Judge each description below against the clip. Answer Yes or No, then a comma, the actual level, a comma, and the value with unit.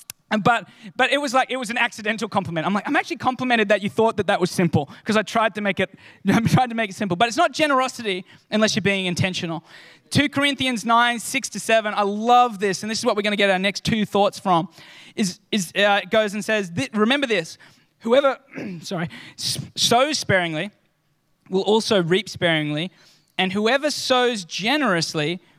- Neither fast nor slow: Yes, average, 190 wpm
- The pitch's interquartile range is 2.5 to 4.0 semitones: No, average, 4.5 semitones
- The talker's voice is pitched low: No, high, 210 Hz